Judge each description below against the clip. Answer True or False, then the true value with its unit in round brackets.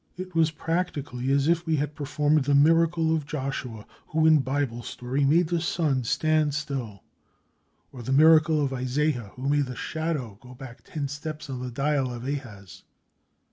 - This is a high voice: False (145 Hz)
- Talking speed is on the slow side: False (175 wpm)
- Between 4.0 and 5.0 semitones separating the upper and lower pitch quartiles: False (3.4 semitones)